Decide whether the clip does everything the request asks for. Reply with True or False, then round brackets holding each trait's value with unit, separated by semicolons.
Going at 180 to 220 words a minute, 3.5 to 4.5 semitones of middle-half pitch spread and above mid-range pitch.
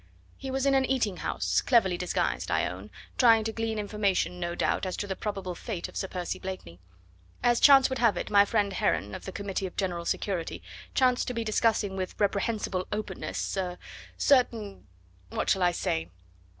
True (190 wpm; 3.8 semitones; 200 Hz)